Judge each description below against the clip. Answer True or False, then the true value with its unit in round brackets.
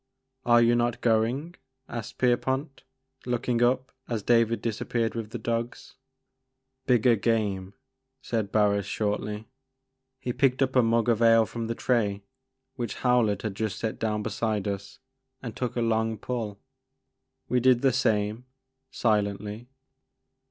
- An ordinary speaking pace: True (160 wpm)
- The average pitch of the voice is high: False (115 Hz)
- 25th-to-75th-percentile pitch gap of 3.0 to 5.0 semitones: False (2.4 semitones)